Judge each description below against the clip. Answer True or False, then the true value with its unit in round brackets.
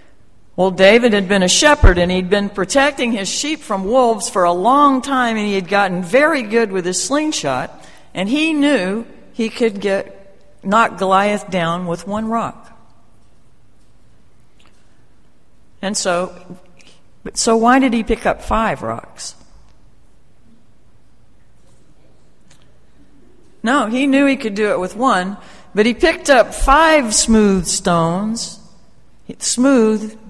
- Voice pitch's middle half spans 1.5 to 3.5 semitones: False (4.7 semitones)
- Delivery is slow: True (130 wpm)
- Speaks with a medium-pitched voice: False (215 Hz)